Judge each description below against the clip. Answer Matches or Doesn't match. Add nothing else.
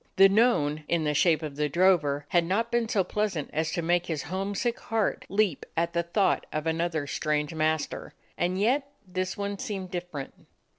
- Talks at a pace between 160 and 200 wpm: Matches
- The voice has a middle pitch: Matches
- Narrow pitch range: Doesn't match